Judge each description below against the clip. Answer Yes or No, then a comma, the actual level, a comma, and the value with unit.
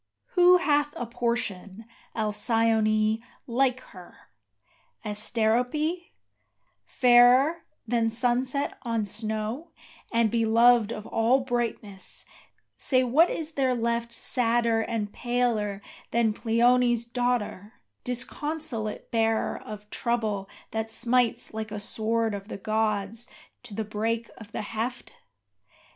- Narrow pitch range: Yes, narrow, 2.3 semitones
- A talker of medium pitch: No, high, 230 Hz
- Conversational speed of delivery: No, slow, 110 wpm